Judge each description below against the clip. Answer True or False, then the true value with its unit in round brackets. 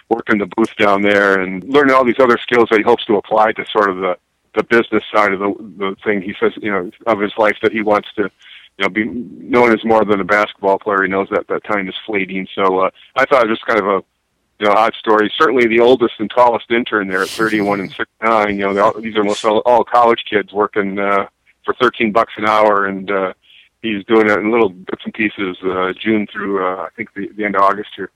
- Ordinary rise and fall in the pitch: False (2.2 semitones)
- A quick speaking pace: True (255 wpm)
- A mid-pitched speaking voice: False (105 Hz)